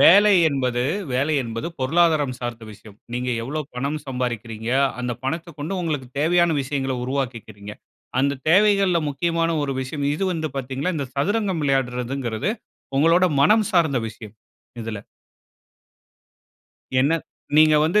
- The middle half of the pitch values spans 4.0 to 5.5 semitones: Yes, average, 4.9 semitones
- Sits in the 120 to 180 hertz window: Yes, medium, 140 Hz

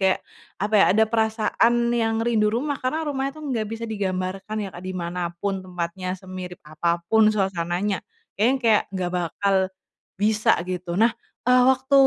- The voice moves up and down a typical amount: Yes, average, 3.7 semitones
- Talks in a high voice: Yes, high, 205 Hz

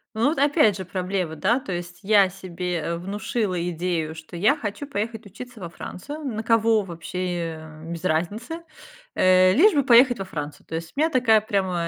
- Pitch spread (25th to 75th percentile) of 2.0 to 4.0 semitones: No, average, 4.8 semitones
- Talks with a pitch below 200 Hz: Yes, high, 190 Hz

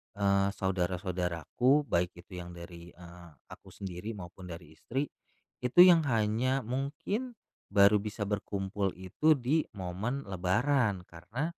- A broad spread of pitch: Yes, wide, 6.4 semitones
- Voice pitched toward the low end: Yes, low, 100 Hz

